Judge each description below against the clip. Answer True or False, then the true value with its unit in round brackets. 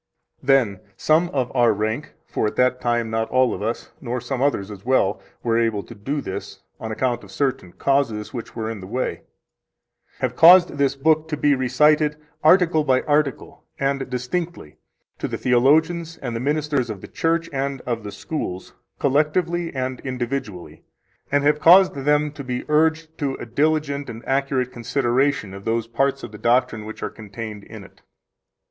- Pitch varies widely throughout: False (4.3 semitones)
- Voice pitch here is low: True (130 Hz)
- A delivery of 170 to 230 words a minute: True (180 wpm)